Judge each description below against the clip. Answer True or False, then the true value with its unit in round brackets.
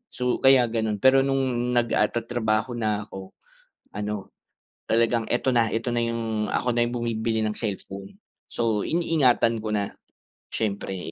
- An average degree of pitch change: False (2.2 semitones)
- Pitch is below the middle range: True (115 Hz)